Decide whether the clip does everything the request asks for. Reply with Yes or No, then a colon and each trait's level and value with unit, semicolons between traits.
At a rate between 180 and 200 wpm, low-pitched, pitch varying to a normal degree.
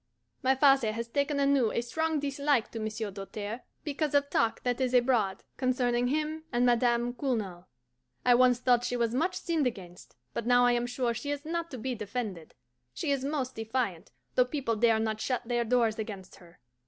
No: average, 190 wpm; high, 245 Hz; average, 3.5 semitones